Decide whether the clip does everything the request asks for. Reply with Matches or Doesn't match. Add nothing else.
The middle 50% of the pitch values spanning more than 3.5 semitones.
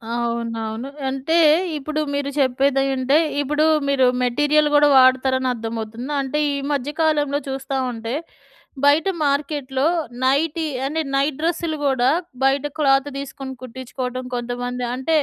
Doesn't match